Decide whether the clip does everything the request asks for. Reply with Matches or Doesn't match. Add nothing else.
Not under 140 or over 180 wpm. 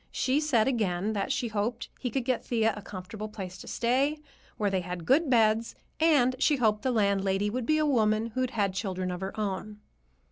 Doesn't match